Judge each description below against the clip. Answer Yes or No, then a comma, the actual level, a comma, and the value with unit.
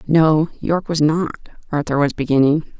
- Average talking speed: Yes, average, 150 wpm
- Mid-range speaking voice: Yes, medium, 155 Hz